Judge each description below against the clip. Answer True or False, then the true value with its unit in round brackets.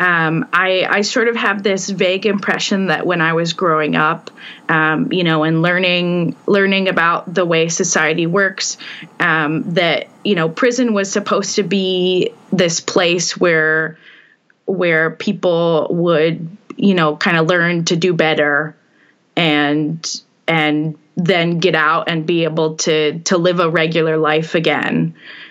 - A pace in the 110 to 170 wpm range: True (150 wpm)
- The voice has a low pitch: False (175 Hz)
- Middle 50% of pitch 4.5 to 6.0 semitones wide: False (3.2 semitones)